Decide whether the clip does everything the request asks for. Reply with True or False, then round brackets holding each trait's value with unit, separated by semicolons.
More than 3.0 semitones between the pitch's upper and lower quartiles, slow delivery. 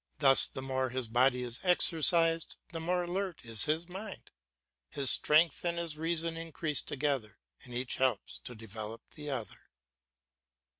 False (4.8 semitones; 150 wpm)